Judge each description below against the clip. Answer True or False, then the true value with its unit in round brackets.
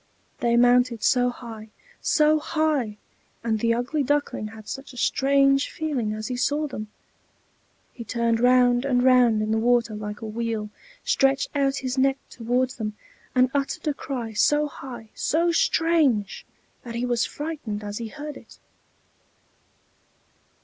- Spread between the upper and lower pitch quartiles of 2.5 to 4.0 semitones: True (3.5 semitones)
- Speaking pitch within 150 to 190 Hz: False (245 Hz)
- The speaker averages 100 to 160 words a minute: True (150 wpm)